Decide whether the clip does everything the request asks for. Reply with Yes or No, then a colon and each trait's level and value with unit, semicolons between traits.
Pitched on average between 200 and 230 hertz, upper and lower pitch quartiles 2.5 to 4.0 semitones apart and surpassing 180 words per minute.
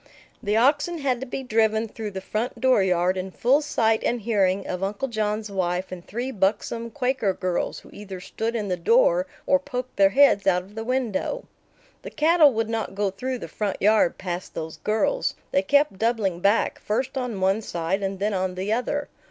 No: high, 215 Hz; average, 4.8 semitones; average, 195 wpm